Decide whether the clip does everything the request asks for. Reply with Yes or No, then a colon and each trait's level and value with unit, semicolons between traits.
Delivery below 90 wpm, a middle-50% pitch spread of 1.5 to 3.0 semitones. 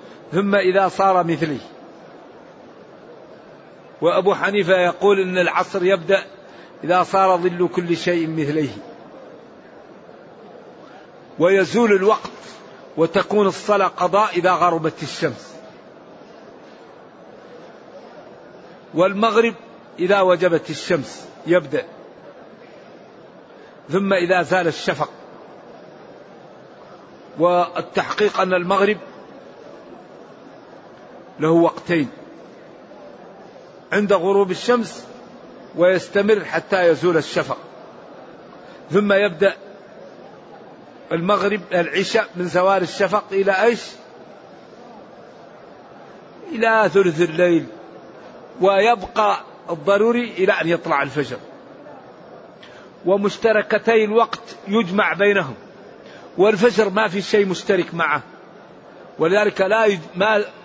Yes: average, 75 wpm; average, 2.7 semitones